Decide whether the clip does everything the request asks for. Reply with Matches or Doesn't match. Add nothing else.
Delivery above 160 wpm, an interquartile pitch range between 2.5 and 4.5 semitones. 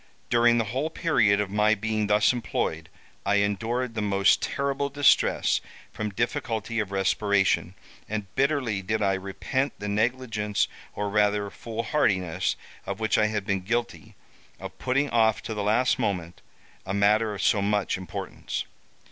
Doesn't match